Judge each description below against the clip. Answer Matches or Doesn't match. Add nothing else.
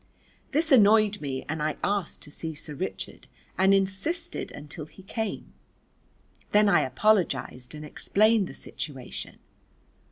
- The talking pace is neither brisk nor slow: Doesn't match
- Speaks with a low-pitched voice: Doesn't match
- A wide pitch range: Matches